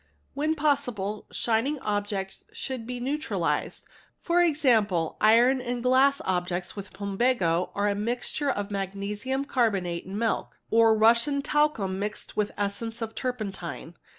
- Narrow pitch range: No, average, 4.5 semitones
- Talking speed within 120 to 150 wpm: Yes, average, 145 wpm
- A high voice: Yes, high, 225 Hz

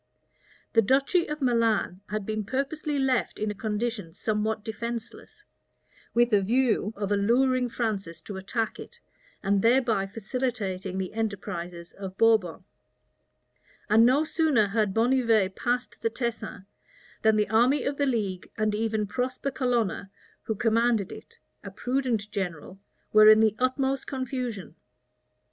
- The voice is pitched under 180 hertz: No, high, 225 Hz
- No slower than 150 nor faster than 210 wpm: No, slow, 135 wpm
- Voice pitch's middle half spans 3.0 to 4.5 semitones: Yes, average, 3.7 semitones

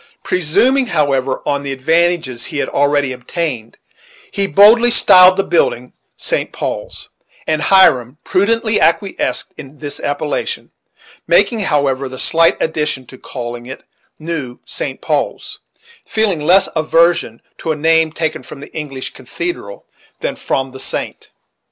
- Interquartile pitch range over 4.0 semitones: Yes, average, 4.9 semitones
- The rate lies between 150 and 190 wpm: No, slow, 135 wpm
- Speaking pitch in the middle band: Yes, medium, 155 Hz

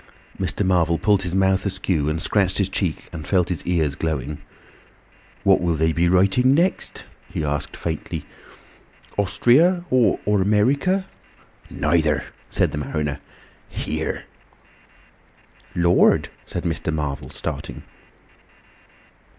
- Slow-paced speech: Yes, slow, 115 wpm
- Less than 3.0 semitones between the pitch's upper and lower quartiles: No, average, 4.4 semitones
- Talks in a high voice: No, very low, 90 Hz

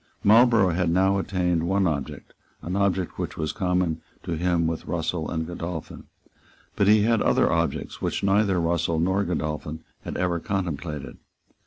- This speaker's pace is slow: No, average, 155 wpm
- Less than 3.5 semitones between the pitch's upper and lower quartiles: Yes, average, 2.9 semitones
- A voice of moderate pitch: No, very low, 90 Hz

